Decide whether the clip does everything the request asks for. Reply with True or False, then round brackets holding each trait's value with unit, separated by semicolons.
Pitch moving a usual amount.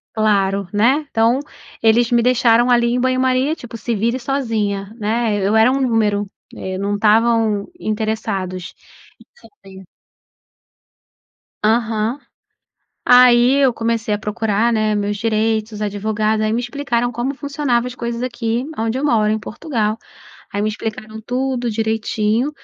False (2.3 semitones)